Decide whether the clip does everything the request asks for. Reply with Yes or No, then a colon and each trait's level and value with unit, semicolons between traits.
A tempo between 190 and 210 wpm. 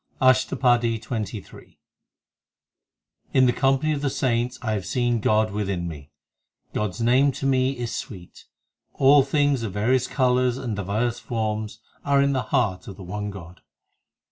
No: average, 160 wpm